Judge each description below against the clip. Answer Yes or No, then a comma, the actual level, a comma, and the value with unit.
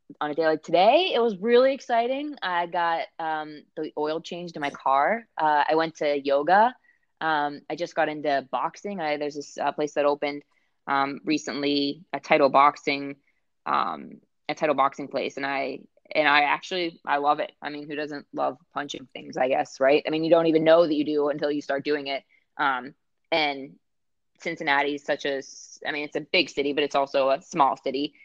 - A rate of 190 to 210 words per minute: Yes, fast, 205 wpm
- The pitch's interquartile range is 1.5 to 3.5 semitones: Yes, average, 2.7 semitones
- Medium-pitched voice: Yes, medium, 150 Hz